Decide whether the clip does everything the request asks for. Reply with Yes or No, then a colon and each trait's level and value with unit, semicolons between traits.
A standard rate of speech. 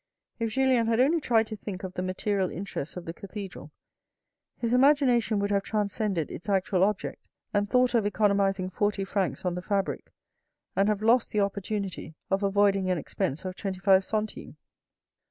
Yes: average, 175 wpm